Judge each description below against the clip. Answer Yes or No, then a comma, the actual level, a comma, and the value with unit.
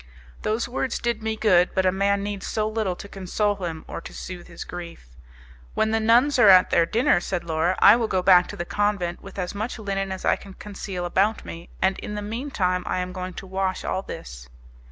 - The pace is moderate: No, fast, 230 wpm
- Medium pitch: No, high, 195 Hz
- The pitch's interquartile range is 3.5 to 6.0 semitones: No, average, 2.9 semitones